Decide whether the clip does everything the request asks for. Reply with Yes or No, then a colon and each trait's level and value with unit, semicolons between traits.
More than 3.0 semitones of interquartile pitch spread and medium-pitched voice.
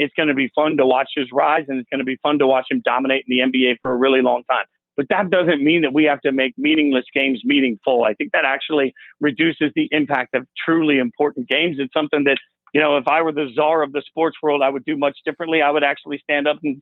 No: narrow, 2.4 semitones; medium, 145 Hz